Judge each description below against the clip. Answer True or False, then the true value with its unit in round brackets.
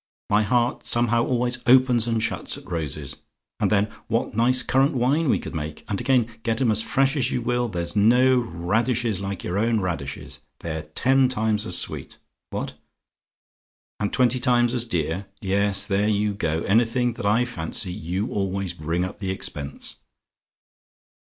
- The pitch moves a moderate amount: True (4.7 semitones)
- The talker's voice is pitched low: True (110 Hz)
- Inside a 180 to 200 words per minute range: False (165 wpm)